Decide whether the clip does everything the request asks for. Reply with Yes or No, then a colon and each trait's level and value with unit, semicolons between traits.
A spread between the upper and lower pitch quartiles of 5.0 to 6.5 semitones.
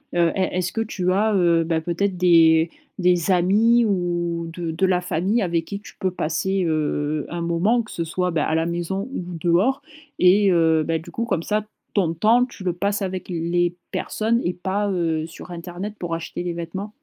No: average, 2.8 semitones